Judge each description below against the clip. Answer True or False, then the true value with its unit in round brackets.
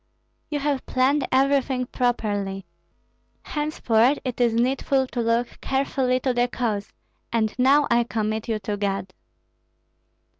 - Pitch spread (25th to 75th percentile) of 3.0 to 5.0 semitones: True (3.3 semitones)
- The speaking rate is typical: False (125 wpm)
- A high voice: True (245 Hz)